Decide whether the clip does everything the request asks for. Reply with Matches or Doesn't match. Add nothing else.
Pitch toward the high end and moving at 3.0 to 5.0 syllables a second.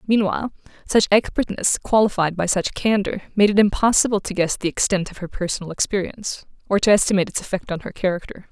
Doesn't match